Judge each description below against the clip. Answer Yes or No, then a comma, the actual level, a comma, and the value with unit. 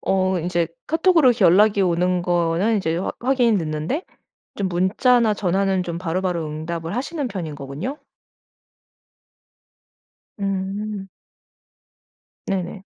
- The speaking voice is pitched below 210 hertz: Yes, high, 190 Hz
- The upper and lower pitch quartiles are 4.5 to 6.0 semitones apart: No, average, 3.8 semitones